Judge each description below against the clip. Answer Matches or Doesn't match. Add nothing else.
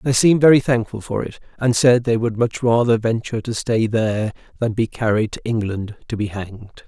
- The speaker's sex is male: Matches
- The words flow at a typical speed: Doesn't match